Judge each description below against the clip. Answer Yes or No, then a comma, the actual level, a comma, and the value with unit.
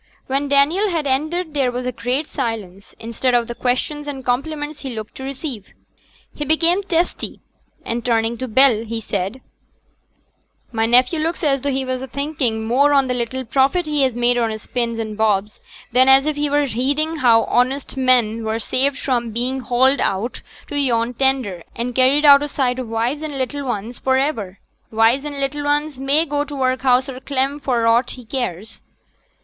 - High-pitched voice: Yes, very high, 260 Hz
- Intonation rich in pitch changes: No, average, 3.4 semitones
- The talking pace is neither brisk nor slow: Yes, average, 190 wpm